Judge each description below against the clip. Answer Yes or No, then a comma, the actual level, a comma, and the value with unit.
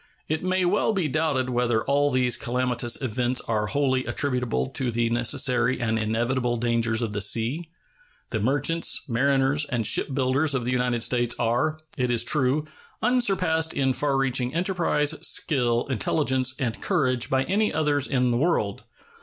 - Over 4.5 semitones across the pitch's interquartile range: No, average, 3.6 semitones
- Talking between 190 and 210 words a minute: No, average, 155 wpm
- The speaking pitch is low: Yes, low, 130 Hz